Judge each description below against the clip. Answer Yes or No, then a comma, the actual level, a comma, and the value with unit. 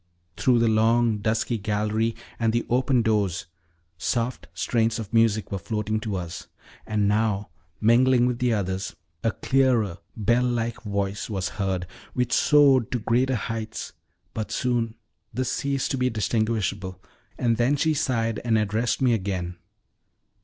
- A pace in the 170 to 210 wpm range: No, average, 145 wpm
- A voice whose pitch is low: Yes, low, 115 Hz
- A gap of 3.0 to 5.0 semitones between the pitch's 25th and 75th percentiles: No, narrow, 2.6 semitones